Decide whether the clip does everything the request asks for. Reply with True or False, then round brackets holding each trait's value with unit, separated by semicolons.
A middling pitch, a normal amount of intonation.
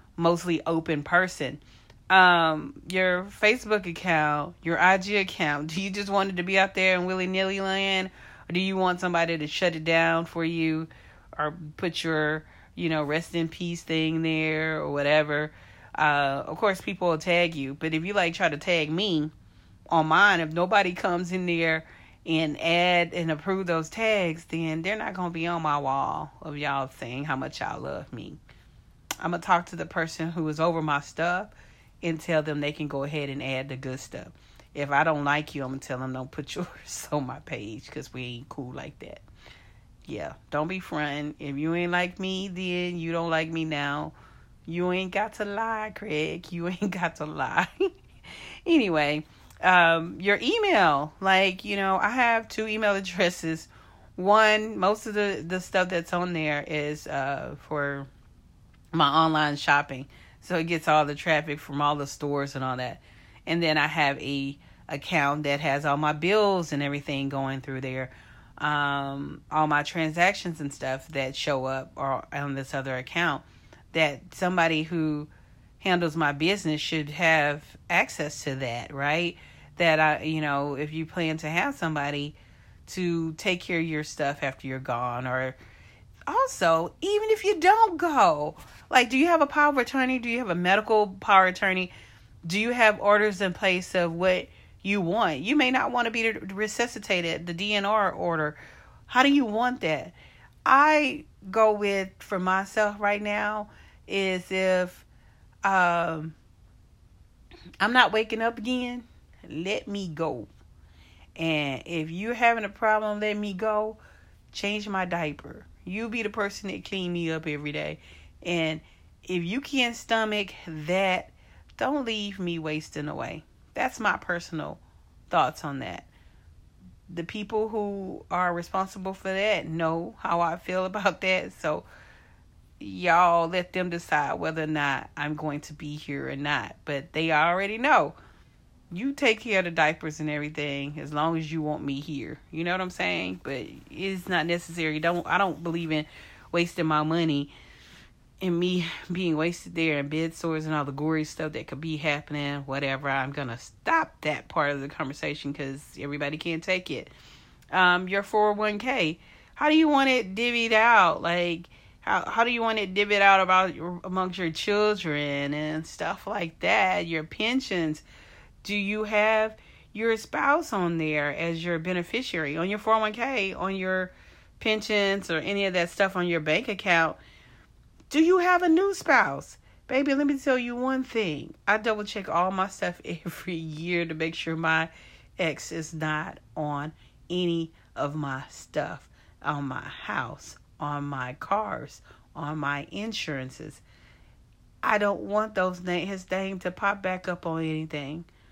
True (165 Hz; 4.7 semitones)